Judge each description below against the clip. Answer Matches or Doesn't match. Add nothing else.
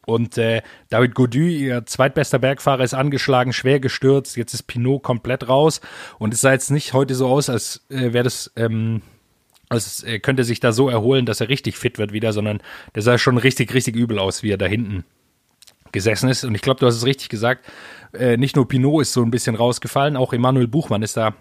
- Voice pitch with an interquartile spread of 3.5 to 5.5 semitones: Doesn't match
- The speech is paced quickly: Matches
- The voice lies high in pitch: Doesn't match